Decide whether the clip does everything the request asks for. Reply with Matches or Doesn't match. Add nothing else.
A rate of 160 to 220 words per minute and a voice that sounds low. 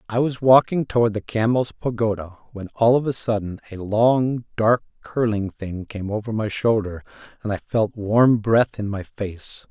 Matches